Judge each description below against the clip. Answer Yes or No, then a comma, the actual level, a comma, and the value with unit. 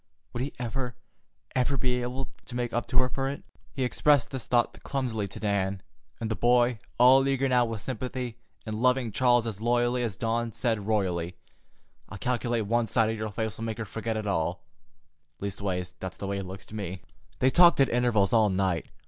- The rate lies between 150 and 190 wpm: No, average, 200 wpm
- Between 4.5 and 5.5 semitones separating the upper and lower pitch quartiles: No, average, 3.5 semitones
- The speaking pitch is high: No, low, 115 Hz